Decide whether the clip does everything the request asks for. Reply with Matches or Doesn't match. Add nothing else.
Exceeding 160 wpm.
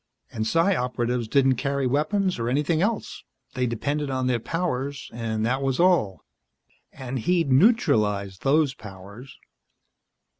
Doesn't match